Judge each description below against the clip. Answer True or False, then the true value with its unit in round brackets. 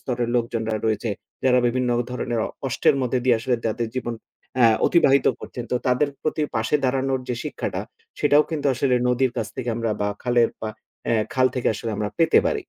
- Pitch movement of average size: False (2.2 semitones)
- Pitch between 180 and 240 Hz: False (125 Hz)